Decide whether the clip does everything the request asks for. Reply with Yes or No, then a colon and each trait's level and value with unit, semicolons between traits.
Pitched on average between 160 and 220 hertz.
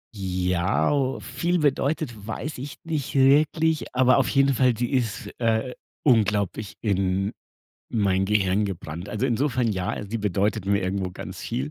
No: low, 110 Hz